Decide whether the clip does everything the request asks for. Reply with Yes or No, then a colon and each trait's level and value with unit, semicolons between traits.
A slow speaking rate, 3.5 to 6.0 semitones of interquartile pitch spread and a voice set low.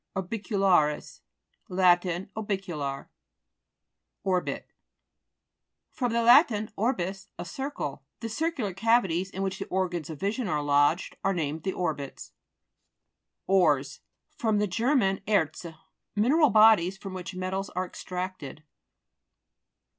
No: slow, 110 wpm; average, 3.9 semitones; high, 190 Hz